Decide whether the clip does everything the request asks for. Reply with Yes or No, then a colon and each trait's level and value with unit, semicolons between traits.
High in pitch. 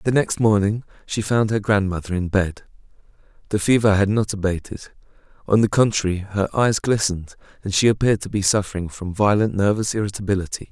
No: low, 100 Hz